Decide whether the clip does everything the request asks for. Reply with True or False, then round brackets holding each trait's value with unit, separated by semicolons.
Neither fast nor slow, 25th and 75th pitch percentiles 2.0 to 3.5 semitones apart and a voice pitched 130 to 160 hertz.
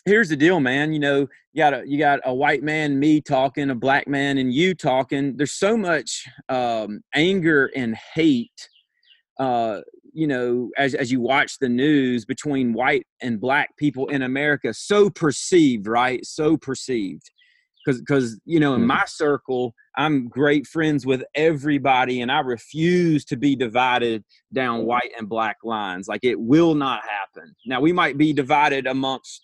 True (170 wpm; 3.0 semitones; 140 Hz)